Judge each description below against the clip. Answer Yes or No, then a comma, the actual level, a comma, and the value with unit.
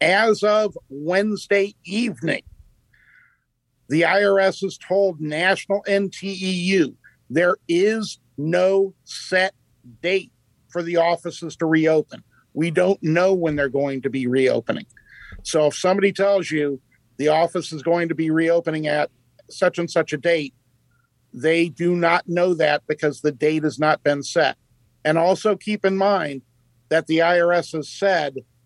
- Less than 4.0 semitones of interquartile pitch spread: No, average, 4.5 semitones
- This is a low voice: No, medium, 165 Hz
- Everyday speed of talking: Yes, average, 145 wpm